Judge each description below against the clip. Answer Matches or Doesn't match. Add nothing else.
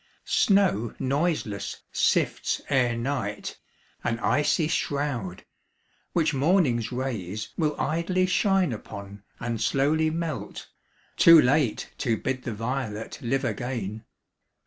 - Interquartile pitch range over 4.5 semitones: Matches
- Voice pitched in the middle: Doesn't match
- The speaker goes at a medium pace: Doesn't match